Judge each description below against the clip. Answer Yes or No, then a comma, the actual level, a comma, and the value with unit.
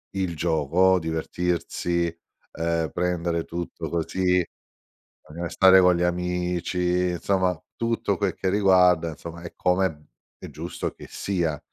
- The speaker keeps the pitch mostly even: Yes, narrow, 1.7 semitones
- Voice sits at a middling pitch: No, very low, 90 Hz